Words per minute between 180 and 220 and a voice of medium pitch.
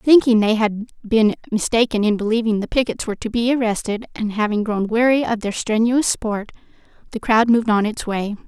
No: average, 190 wpm; high, 225 Hz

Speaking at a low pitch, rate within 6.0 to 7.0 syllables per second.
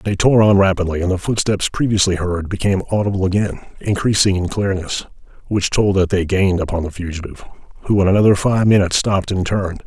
Yes: very low, 95 Hz; 6.5 syllables/s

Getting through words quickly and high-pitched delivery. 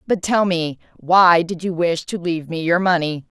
No: fast, 215 wpm; medium, 170 Hz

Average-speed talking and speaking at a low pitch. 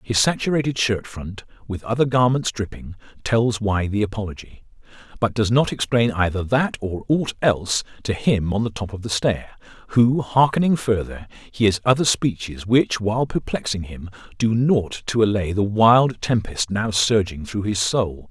Yes: average, 165 wpm; low, 110 Hz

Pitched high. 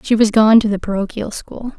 Yes: high, 215 Hz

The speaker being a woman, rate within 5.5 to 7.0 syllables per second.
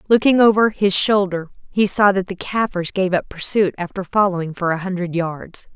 No: female; 5.1 syllables/s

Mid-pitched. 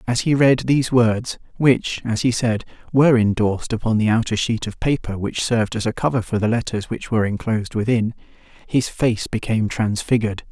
No: low, 115 Hz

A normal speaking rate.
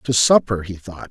No: fast, 215 wpm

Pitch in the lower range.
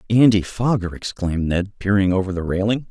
Yes: low, 100 Hz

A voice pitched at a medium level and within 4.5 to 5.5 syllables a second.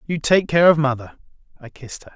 No: medium, 145 Hz; 6.6 syllables/s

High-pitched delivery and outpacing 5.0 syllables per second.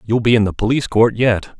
No: low, 115 Hz; 6.2 syllables/s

